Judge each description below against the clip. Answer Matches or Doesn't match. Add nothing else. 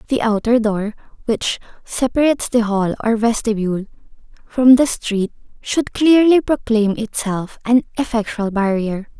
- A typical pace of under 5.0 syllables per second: Matches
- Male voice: Doesn't match